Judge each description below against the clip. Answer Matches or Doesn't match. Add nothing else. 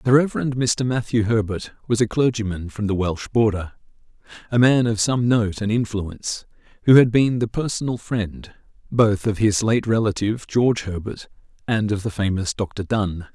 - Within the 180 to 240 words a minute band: Doesn't match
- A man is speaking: Matches